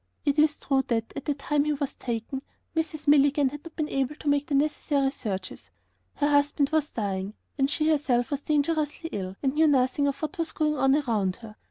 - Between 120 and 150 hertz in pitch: No, very high, 285 Hz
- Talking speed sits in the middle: No, fast, 210 wpm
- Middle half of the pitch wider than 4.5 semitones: No, narrow, 2.6 semitones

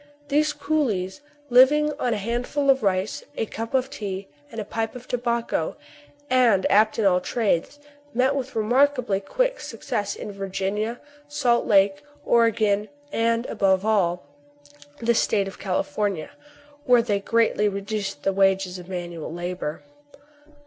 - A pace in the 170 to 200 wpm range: No, average, 145 wpm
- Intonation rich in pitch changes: No, average, 4.2 semitones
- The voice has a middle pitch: No, high, 215 Hz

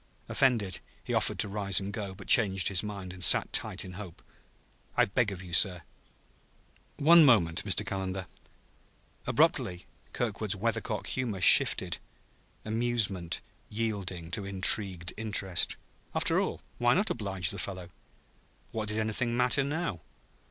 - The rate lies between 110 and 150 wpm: Yes, average, 140 wpm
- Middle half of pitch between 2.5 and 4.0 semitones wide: Yes, average, 3.4 semitones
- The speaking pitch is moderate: No, low, 100 Hz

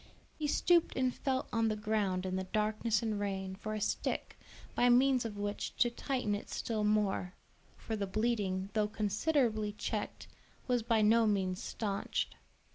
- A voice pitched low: No, high, 215 Hz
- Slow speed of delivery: No, average, 165 wpm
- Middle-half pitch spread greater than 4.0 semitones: No, narrow, 2.5 semitones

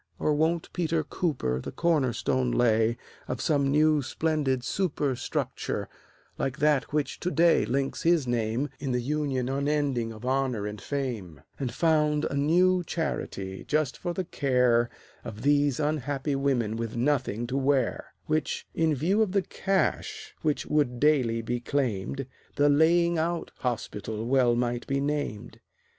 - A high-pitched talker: No, medium, 140 Hz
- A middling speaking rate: Yes, average, 150 wpm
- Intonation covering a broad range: No, average, 4.1 semitones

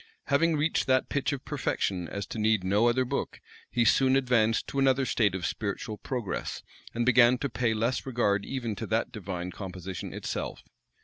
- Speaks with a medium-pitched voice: No, low, 115 Hz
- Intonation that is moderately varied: Yes, average, 4.4 semitones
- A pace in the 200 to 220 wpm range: No, average, 180 wpm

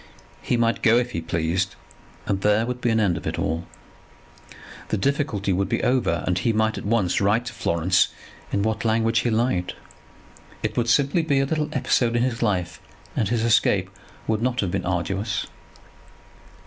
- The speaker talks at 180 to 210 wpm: Yes, average, 185 wpm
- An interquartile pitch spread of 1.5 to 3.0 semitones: No, average, 4.1 semitones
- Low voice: Yes, low, 110 Hz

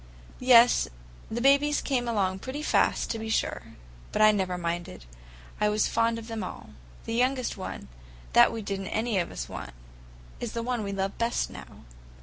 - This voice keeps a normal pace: Yes, average, 185 wpm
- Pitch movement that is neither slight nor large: Yes, average, 3.8 semitones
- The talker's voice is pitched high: Yes, high, 225 Hz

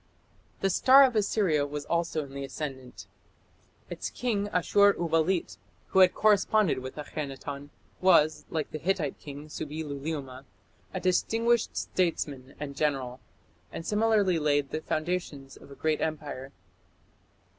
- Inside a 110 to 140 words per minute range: Yes, slow, 135 wpm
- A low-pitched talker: No, medium, 155 Hz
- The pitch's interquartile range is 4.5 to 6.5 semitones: Yes, average, 4.9 semitones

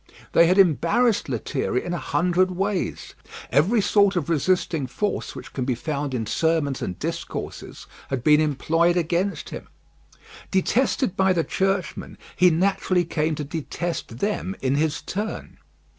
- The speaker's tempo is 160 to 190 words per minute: No, average, 145 wpm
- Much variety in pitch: No, average, 4.3 semitones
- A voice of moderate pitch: Yes, medium, 170 Hz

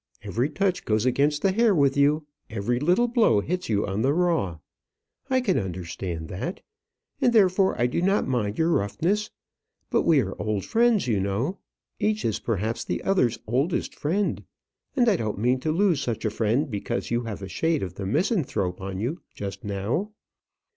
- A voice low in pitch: Yes, low, 130 Hz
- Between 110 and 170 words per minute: No, average, 180 wpm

